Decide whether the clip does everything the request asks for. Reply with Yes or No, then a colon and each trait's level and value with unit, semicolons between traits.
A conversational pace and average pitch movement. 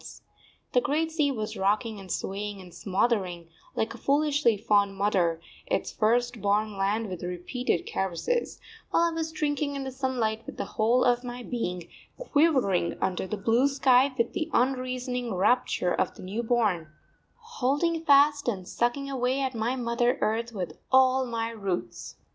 Yes: average, 160 wpm; average, 5.0 semitones